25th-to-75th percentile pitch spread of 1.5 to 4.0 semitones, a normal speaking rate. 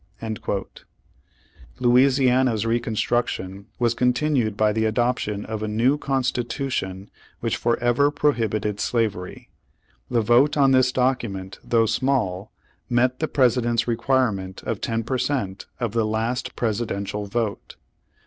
No: average, 3.2 semitones; slow, 120 wpm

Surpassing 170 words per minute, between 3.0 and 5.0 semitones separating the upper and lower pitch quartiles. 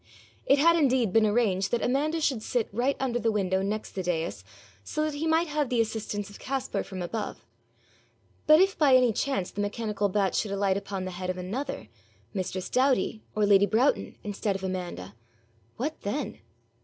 No: average, 185 wpm; wide, 5.6 semitones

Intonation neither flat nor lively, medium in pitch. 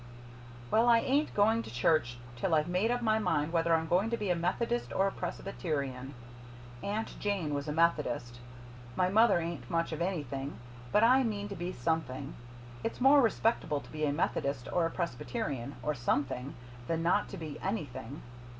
No: wide, 6.4 semitones; medium, 165 Hz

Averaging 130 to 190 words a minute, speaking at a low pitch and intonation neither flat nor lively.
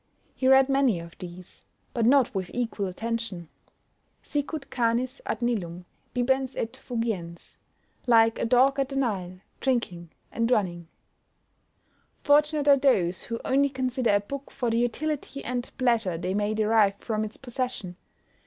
No: average, 145 wpm; high, 235 Hz; average, 4.9 semitones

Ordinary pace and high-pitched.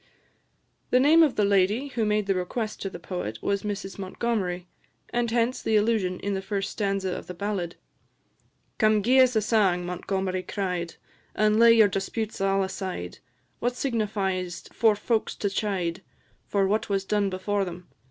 Yes: average, 170 wpm; high, 200 Hz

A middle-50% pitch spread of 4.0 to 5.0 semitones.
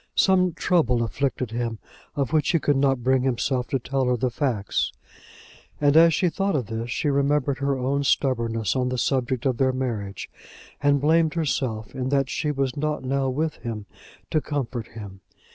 No: average, 3.1 semitones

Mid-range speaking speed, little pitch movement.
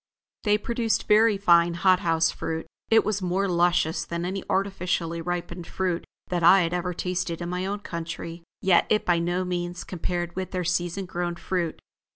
Yes: average, 180 wpm; narrow, 1.7 semitones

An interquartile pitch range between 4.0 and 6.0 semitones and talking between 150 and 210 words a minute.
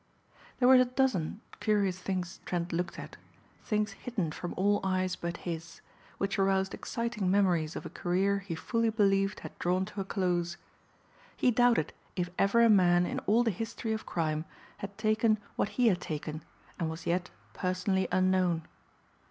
No: average, 3.3 semitones; average, 170 wpm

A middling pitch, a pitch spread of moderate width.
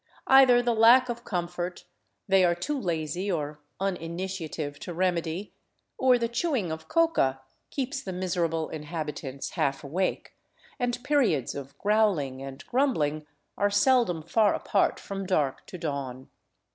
No: medium, 180 Hz; wide, 6.7 semitones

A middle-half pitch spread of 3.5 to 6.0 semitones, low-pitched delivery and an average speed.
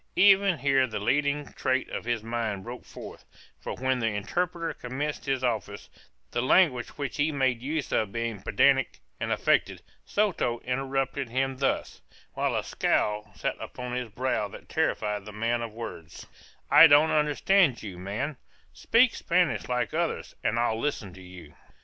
Yes: average, 4.6 semitones; low, 125 Hz; average, 160 wpm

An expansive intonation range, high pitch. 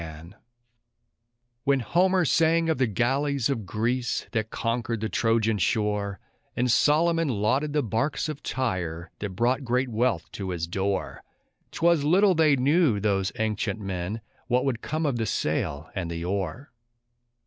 No: wide, 5.9 semitones; low, 120 Hz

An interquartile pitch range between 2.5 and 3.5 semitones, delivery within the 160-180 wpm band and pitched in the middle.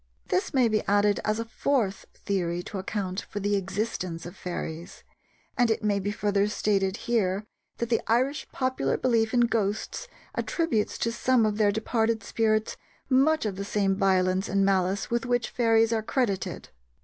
No: average, 3.0 semitones; average, 170 wpm; high, 210 Hz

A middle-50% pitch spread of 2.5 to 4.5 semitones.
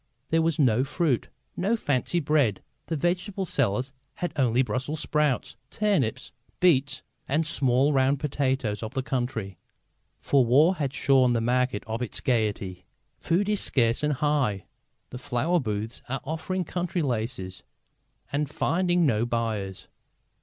No: average, 5.2 semitones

